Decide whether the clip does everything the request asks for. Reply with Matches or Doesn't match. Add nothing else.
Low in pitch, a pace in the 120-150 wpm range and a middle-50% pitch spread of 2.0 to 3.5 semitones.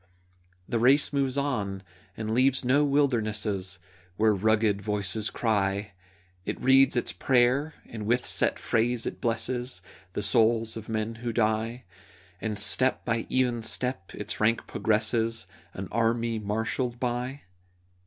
Matches